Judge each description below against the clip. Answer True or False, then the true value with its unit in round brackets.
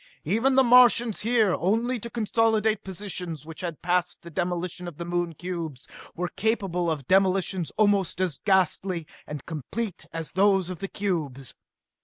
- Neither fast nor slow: True (155 wpm)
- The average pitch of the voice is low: False (185 Hz)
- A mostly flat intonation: False (3.7 semitones)